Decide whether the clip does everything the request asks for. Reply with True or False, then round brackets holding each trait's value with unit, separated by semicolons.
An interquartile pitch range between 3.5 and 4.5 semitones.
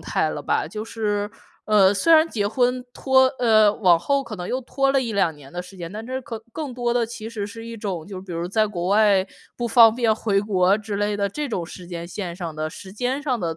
True (4.2 semitones)